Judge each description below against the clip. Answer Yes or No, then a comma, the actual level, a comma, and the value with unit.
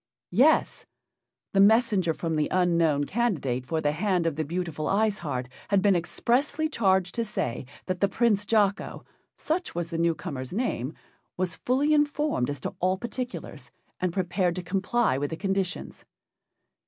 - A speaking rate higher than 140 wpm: Yes, average, 160 wpm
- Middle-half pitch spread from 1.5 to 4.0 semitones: No, average, 5.1 semitones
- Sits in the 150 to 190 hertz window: Yes, medium, 185 Hz